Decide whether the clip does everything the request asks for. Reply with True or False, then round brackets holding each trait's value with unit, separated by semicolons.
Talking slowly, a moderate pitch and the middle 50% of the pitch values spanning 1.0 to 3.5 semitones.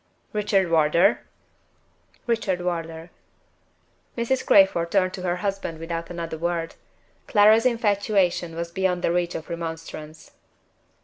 True (115 wpm; 175 Hz; 3.1 semitones)